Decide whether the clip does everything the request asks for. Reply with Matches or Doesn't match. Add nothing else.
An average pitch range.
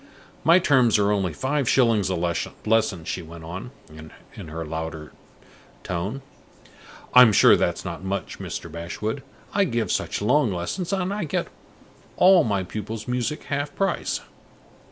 Doesn't match